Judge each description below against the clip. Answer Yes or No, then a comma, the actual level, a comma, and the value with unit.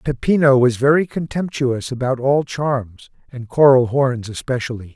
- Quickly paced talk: No, slow, 135 wpm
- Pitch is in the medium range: No, low, 130 Hz